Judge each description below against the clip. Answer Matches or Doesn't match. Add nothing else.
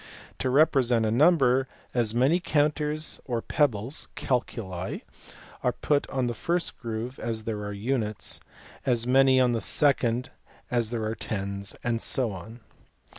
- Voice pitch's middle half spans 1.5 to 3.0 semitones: Doesn't match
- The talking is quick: Doesn't match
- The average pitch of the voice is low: Matches